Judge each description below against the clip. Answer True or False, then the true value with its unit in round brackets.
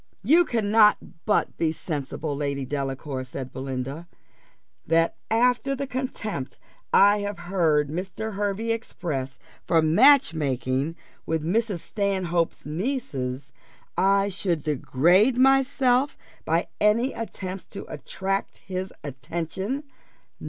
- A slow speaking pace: True (110 wpm)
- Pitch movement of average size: False (6.9 semitones)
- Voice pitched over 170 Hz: True (185 Hz)